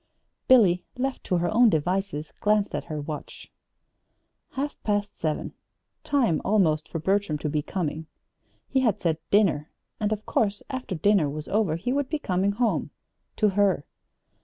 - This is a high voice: Yes, high, 195 Hz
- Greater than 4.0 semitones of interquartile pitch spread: Yes, average, 5.3 semitones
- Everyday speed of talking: Yes, average, 160 wpm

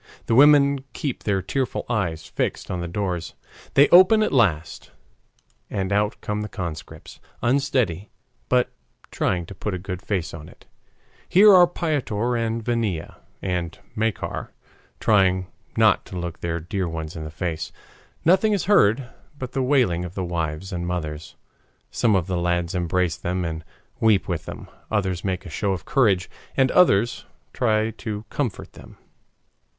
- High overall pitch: No, very low, 95 Hz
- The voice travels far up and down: Yes, wide, 5.7 semitones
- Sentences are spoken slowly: No, average, 160 wpm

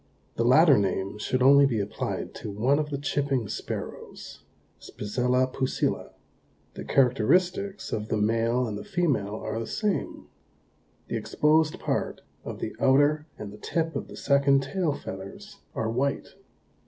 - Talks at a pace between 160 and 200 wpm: No, average, 150 wpm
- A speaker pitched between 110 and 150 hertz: Yes, low, 135 Hz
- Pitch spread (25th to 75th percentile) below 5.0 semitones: No, wide, 5.4 semitones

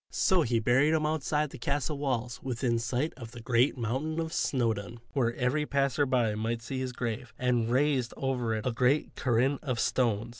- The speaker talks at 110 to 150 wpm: No, average, 190 wpm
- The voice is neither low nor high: No, low, 125 Hz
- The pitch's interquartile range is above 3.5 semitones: No, average, 3.1 semitones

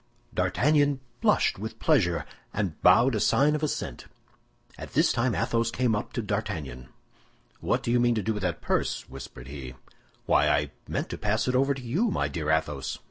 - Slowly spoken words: No, average, 190 wpm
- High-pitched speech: No, low, 110 Hz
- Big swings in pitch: Yes, wide, 7.3 semitones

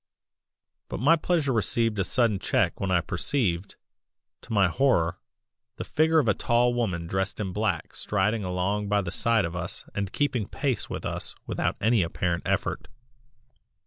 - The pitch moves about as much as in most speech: Yes, average, 4.7 semitones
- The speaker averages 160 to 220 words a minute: Yes, average, 165 wpm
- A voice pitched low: Yes, low, 105 Hz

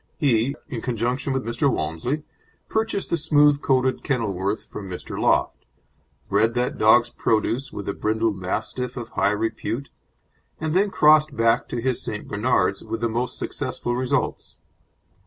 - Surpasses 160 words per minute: No, average, 150 wpm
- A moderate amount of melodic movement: Yes, average, 3.8 semitones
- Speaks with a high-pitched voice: No, low, 120 Hz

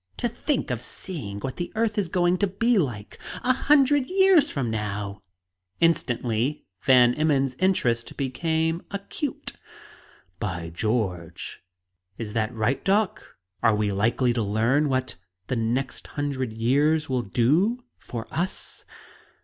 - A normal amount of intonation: No, wide, 8.4 semitones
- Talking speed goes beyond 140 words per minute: No, slow, 135 wpm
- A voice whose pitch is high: No, low, 135 Hz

